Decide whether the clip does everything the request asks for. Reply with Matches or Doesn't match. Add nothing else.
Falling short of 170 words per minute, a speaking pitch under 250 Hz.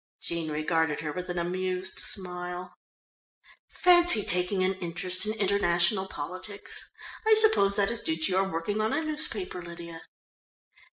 Matches